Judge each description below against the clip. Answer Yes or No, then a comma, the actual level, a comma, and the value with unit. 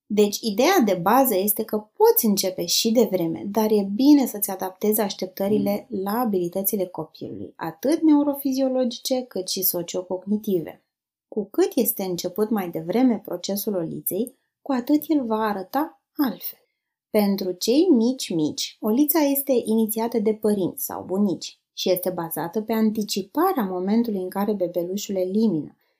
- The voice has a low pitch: No, high, 215 Hz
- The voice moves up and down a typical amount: Yes, average, 4.9 semitones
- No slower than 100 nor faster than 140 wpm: Yes, average, 135 wpm